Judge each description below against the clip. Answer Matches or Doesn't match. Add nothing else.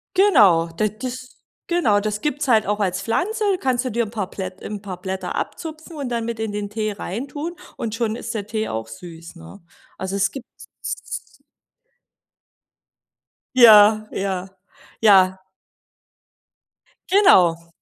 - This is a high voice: Matches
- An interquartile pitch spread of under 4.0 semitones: Doesn't match